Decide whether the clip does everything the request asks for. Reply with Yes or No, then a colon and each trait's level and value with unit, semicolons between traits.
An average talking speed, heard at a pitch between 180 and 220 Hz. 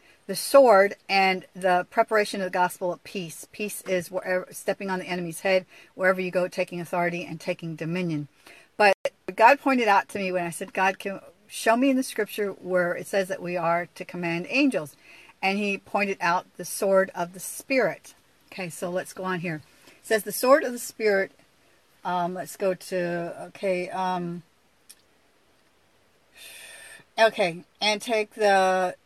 Yes: average, 170 wpm; medium, 185 Hz